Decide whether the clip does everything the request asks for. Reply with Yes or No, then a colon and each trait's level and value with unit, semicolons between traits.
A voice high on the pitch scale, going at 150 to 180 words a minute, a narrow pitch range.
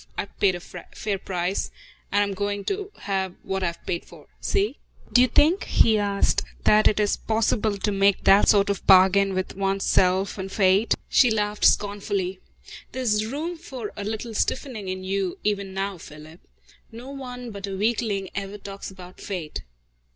Yes: high, 200 Hz; average, 175 wpm; narrow, 2.3 semitones